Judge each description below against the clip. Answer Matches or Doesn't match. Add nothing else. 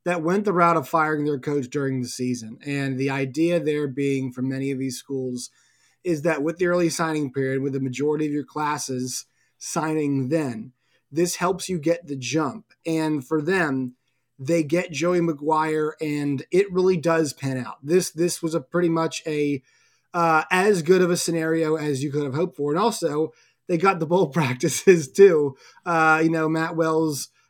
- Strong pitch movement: Doesn't match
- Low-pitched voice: Doesn't match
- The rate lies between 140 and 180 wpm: Doesn't match